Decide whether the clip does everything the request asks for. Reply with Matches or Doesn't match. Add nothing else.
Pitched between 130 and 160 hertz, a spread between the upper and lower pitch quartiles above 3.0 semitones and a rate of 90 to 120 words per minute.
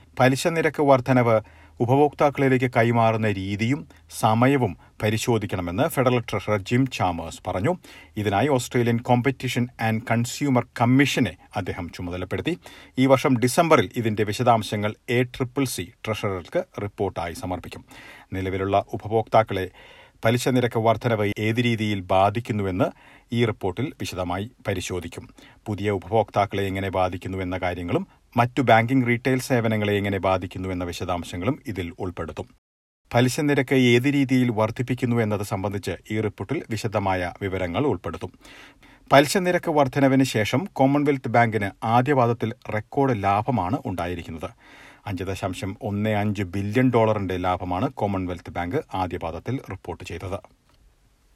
Doesn't match